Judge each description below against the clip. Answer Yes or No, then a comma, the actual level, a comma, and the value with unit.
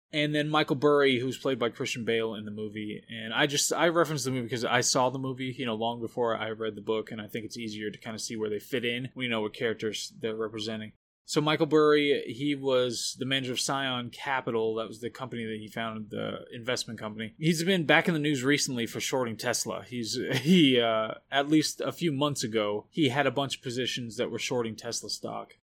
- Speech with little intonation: No, average, 4.0 semitones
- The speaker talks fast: Yes, fast, 240 wpm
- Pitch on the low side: Yes, low, 125 Hz